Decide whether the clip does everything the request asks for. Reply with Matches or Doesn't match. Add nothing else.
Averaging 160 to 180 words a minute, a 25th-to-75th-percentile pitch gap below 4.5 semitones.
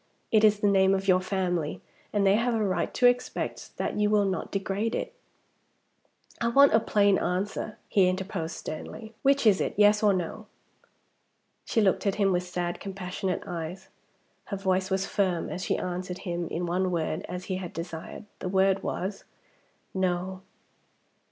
Matches